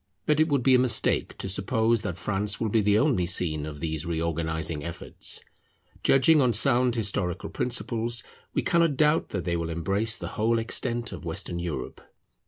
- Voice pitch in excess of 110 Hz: No, low, 105 Hz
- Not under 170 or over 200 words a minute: Yes, average, 180 wpm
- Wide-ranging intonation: Yes, wide, 6.2 semitones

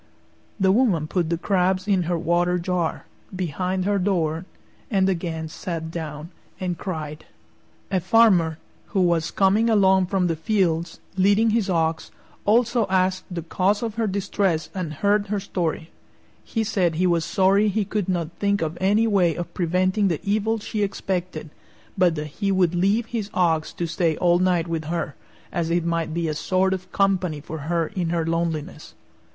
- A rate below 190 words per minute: Yes, average, 175 wpm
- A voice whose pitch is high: No, medium, 180 Hz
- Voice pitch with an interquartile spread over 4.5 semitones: No, average, 3.0 semitones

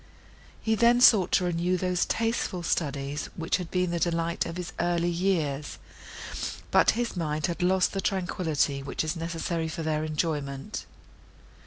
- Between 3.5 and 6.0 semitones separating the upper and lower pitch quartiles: No, average, 2.7 semitones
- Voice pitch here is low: No, medium, 170 Hz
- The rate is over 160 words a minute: No, average, 155 wpm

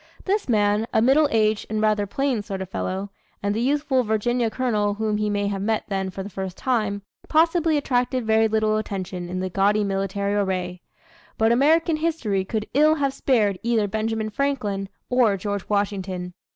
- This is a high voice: Yes, high, 215 Hz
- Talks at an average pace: Yes, average, 180 wpm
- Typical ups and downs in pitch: Yes, average, 3.8 semitones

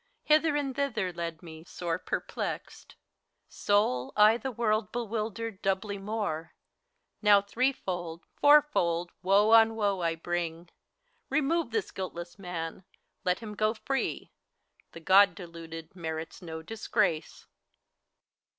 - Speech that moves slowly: Yes, slow, 115 wpm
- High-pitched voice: Yes, high, 195 Hz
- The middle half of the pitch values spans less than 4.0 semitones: No, average, 4.9 semitones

